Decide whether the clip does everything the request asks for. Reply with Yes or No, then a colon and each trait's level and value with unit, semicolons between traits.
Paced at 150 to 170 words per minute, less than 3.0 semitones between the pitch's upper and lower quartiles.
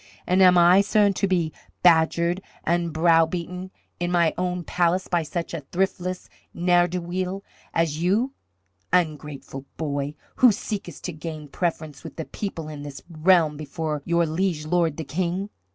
Yes: average, 155 wpm; narrow, 2.5 semitones